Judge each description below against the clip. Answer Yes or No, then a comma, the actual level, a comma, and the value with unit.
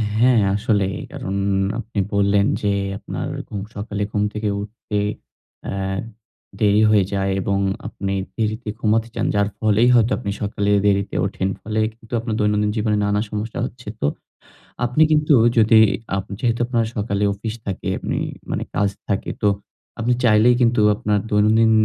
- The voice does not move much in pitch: Yes, narrow, 1.9 semitones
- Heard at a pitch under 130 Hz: Yes, low, 105 Hz